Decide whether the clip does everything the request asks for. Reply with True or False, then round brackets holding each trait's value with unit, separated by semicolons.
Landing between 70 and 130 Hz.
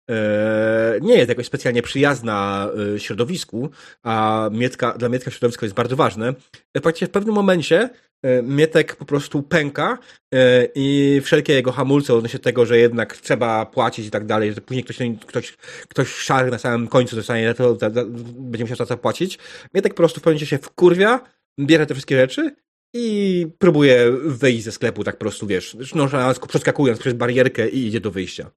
True (125 Hz)